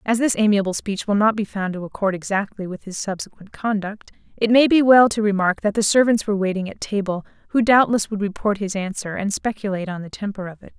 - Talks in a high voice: Yes, high, 205 Hz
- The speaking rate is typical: No, fast, 230 wpm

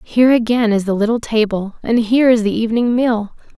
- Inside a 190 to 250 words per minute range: Yes, average, 200 wpm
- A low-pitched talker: No, high, 225 Hz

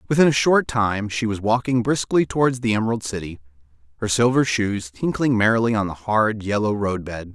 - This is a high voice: No, low, 110 Hz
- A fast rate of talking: No, average, 190 wpm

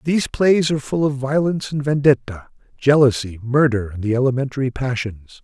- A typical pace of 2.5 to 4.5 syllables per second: No, 5.6 syllables/s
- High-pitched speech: No, low, 135 Hz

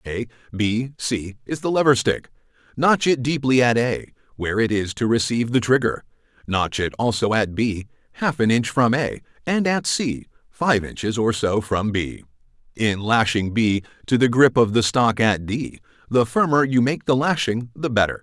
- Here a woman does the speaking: No, male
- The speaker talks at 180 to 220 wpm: Yes, average, 190 wpm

